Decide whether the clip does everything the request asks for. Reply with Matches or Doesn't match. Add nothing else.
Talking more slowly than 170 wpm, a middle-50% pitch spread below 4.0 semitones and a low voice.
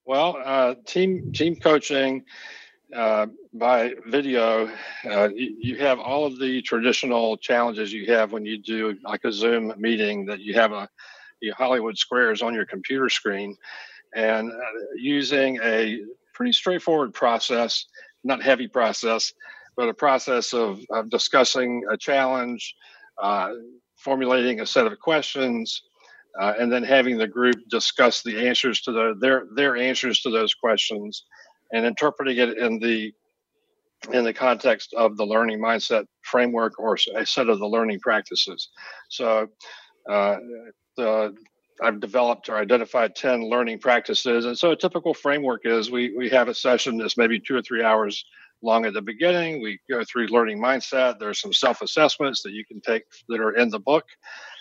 Matches